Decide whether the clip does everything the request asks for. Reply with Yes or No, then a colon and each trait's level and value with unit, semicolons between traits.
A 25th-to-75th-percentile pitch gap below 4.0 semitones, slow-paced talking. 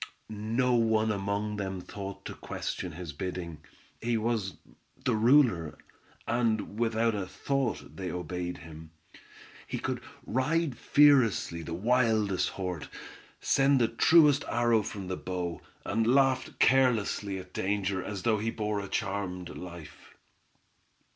No: average, 4.3 semitones; slow, 130 wpm